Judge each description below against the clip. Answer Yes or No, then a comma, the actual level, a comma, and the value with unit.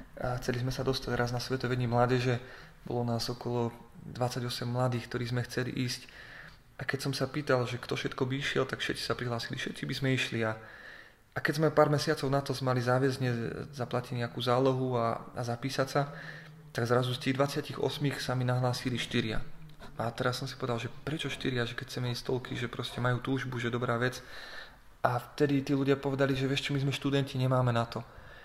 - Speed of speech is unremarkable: No, fast, 200 wpm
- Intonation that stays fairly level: Yes, narrow, 2.2 semitones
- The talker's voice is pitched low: Yes, low, 125 Hz